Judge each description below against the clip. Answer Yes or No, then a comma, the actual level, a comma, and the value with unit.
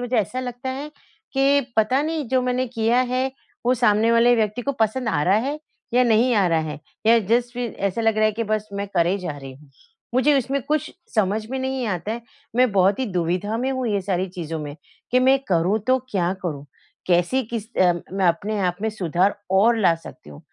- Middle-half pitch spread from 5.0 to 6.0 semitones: Yes, wide, 5.5 semitones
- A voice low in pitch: No, high, 220 Hz